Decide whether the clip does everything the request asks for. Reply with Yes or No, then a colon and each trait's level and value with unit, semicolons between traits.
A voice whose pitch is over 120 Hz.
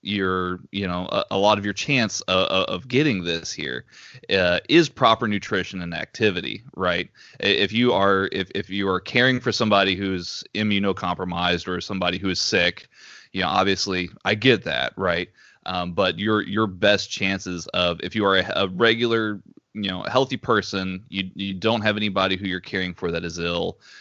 No: very low, 95 Hz